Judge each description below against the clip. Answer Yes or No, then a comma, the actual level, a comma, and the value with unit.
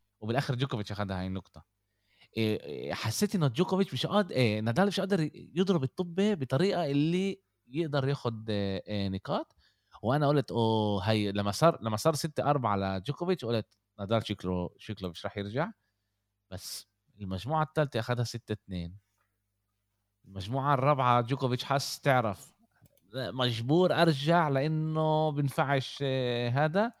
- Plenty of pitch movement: Yes, wide, 7.1 semitones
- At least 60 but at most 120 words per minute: No, average, 130 wpm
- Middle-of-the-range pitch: No, low, 125 Hz